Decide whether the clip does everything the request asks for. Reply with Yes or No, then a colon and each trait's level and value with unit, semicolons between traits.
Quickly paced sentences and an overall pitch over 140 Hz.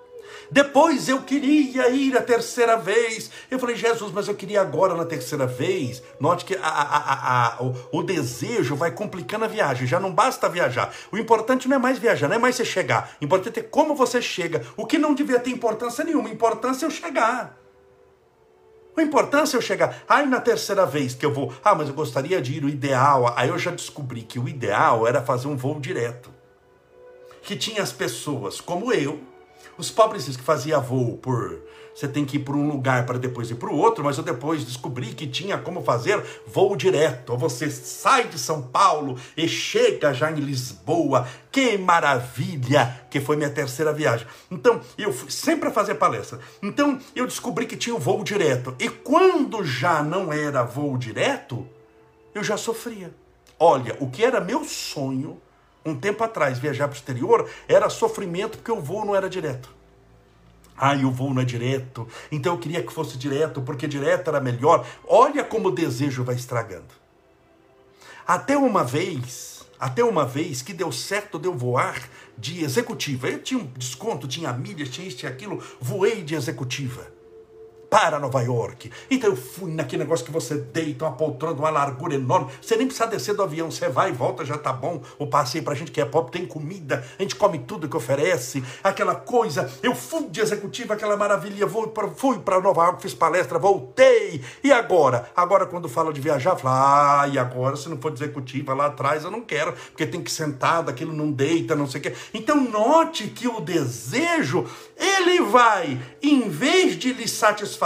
Yes: fast, 195 wpm; medium, 165 Hz